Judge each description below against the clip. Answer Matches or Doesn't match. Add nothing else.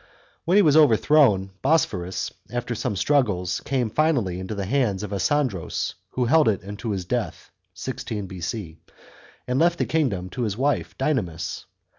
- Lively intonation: Matches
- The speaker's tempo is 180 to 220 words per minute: Doesn't match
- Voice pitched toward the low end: Matches